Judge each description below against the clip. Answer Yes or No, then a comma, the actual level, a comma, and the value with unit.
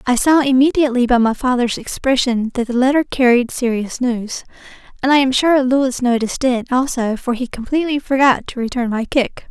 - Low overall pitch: No, very high, 250 Hz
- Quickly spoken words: No, average, 185 wpm